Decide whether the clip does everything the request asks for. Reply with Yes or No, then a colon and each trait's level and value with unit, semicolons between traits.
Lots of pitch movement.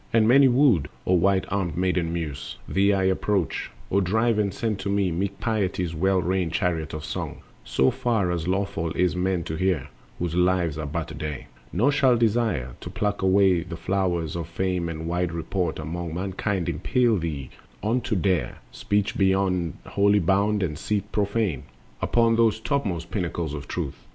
No: average, 3.4 semitones